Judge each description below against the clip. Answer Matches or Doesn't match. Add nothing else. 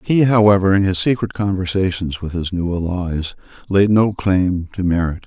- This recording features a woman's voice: Doesn't match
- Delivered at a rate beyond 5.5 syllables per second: Doesn't match